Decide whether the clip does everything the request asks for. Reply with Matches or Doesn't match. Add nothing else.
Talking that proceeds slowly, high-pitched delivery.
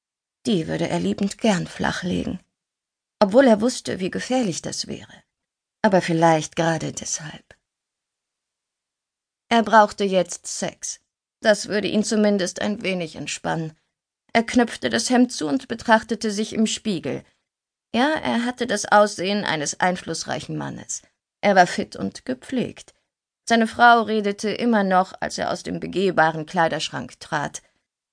Doesn't match